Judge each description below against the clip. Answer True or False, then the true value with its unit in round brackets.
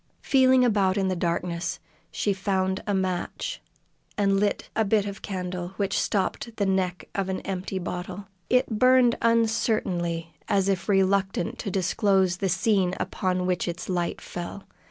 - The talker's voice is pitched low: False (190 Hz)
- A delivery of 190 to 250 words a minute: False (155 wpm)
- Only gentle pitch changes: True (2.2 semitones)